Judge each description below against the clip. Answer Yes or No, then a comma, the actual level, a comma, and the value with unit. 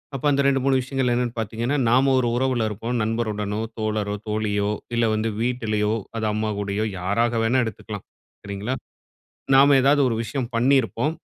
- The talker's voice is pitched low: Yes, low, 115 Hz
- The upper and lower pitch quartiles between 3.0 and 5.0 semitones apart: Yes, average, 3.3 semitones